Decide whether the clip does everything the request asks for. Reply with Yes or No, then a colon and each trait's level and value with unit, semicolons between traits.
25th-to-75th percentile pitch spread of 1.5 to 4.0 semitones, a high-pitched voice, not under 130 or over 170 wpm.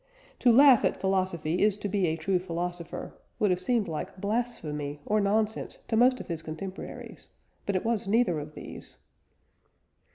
No: average, 4.4 semitones; high, 195 Hz; average, 165 wpm